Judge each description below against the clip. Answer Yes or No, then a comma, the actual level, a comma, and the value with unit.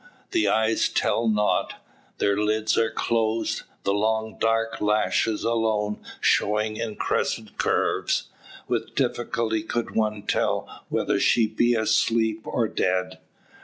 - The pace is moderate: No, slow, 125 wpm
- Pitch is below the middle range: Yes, low, 110 Hz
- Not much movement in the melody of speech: Yes, narrow, 1.1 semitones